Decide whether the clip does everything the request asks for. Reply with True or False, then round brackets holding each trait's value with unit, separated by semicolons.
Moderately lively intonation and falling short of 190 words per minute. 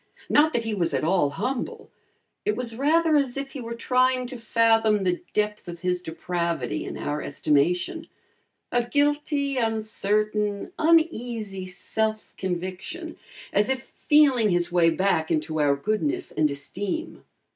False (6.9 semitones; 145 wpm)